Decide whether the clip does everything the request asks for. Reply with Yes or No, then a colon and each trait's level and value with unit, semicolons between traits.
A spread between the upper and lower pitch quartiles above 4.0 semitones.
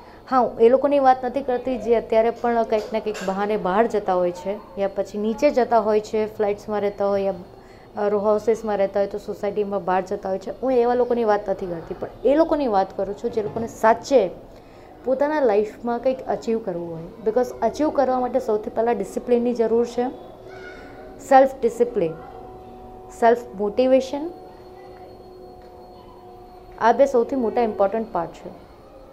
No: average, 3.4 semitones